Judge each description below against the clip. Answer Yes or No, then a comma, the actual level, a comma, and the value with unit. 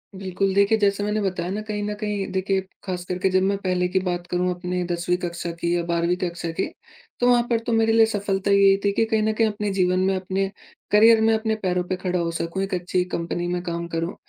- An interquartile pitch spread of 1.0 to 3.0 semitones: Yes, narrow, 2.6 semitones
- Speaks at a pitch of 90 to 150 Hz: No, high, 190 Hz